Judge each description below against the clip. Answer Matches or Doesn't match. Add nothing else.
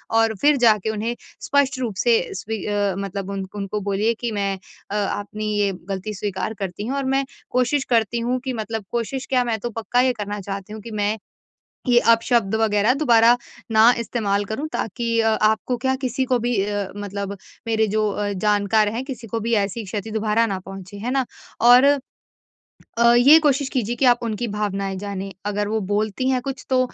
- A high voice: Matches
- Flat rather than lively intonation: Doesn't match